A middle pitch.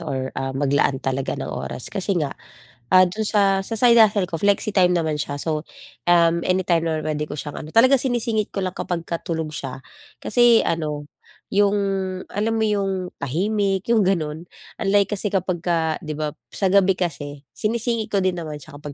Yes: medium, 175 Hz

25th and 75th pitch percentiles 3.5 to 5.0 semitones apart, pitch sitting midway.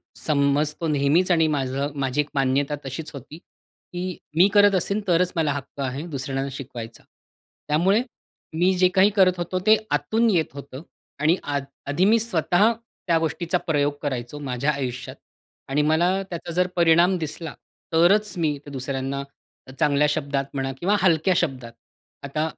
Yes: average, 4.2 semitones; medium, 150 Hz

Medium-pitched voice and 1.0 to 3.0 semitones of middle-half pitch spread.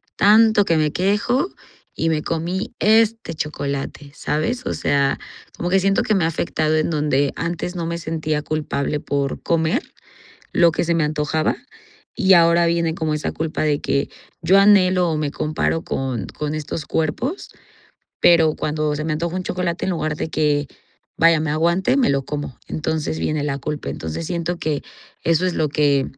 Yes: medium, 160 Hz; average, 2.7 semitones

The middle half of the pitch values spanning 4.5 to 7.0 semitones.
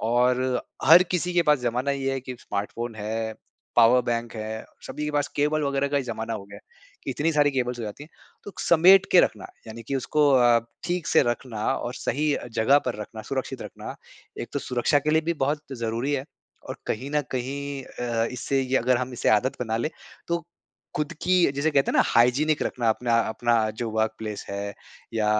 No: average, 4.0 semitones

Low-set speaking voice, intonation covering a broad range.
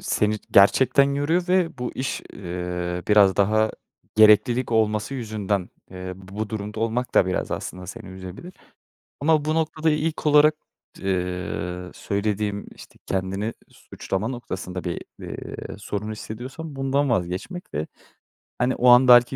Yes: low, 110 Hz; wide, 5.9 semitones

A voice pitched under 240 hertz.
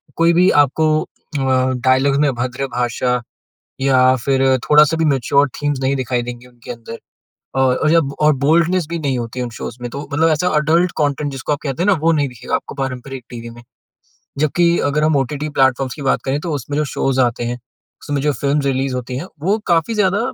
Yes: medium, 140 Hz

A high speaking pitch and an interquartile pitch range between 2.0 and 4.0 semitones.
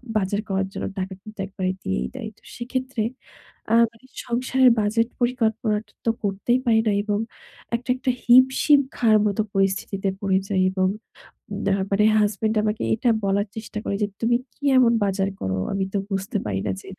Yes: high, 215 Hz; average, 3.4 semitones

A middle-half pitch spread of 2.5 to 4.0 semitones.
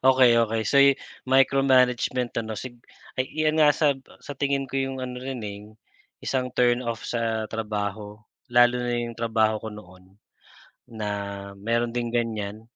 Yes: average, 3.0 semitones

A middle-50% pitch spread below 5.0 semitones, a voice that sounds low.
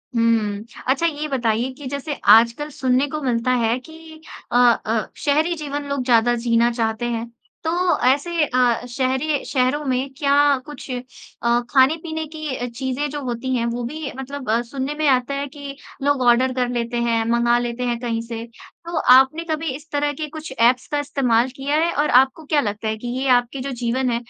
No: average, 3.5 semitones; very high, 260 Hz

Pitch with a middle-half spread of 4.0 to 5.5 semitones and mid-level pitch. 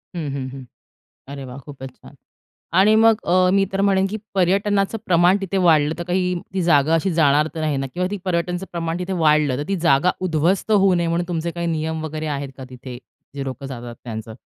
Yes: average, 4.7 semitones; medium, 165 Hz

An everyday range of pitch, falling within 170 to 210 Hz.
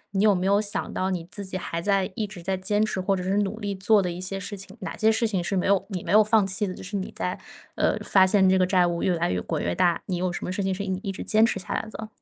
No: narrow, 2.0 semitones; high, 190 Hz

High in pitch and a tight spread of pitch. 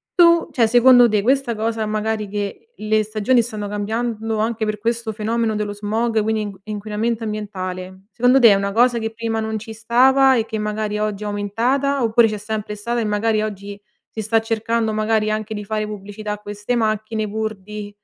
Yes: high, 215 Hz; narrow, 1.5 semitones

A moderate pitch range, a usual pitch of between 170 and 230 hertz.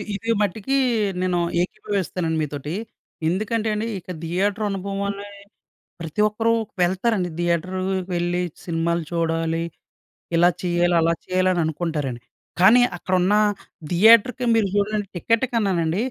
Yes: average, 3.5 semitones; medium, 185 Hz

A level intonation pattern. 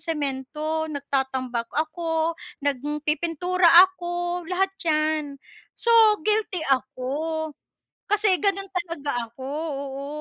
No: average, 3.8 semitones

